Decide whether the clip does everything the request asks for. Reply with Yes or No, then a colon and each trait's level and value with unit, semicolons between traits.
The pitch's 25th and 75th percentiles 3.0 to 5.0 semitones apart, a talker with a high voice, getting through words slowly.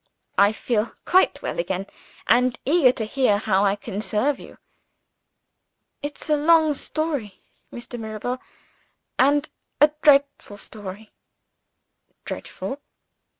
No: wide, 5.5 semitones; high, 245 Hz; slow, 110 wpm